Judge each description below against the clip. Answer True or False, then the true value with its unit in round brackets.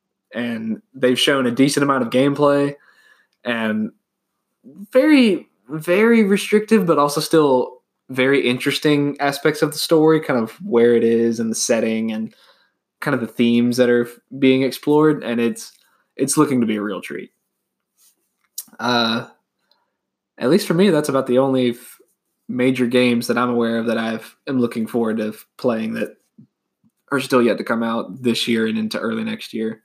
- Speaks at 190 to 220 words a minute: False (165 wpm)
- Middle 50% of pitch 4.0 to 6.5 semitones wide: True (4.7 semitones)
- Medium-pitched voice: False (130 Hz)